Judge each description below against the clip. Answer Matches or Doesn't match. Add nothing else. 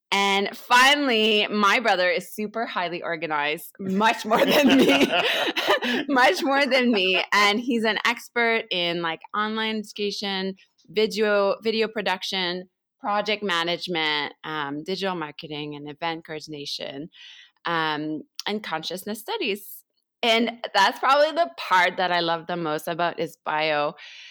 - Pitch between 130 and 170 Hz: Doesn't match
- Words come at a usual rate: Doesn't match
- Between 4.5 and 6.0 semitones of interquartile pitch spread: Matches